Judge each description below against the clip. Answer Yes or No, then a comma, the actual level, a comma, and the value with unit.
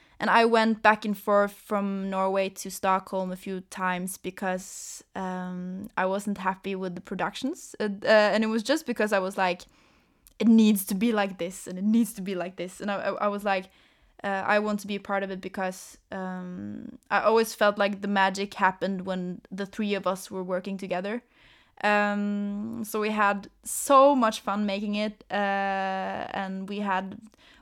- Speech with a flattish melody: Yes, narrow, 2.1 semitones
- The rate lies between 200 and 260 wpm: No, average, 190 wpm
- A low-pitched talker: No, high, 200 Hz